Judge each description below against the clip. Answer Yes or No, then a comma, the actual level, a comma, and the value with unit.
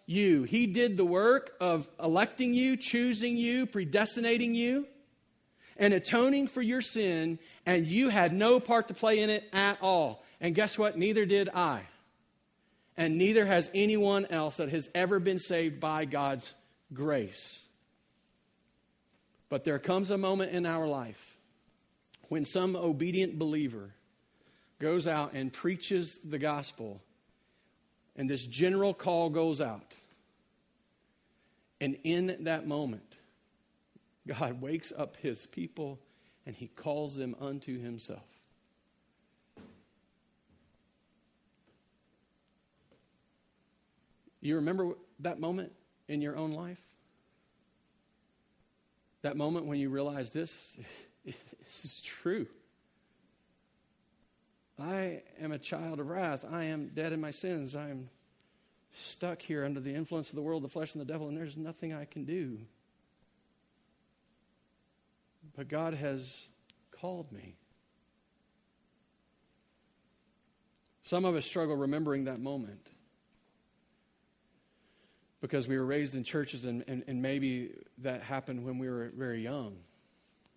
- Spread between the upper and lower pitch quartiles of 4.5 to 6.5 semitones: Yes, average, 5.2 semitones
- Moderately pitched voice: Yes, medium, 160 Hz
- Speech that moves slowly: Yes, slow, 120 wpm